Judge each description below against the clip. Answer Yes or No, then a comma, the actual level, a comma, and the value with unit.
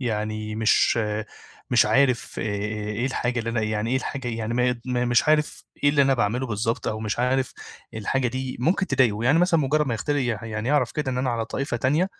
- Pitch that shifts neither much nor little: Yes, average, 3.3 semitones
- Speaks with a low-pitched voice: Yes, low, 125 Hz